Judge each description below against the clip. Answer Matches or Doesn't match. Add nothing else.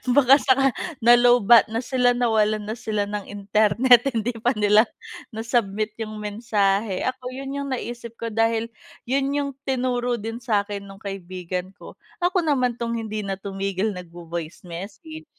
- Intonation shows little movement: Doesn't match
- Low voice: Doesn't match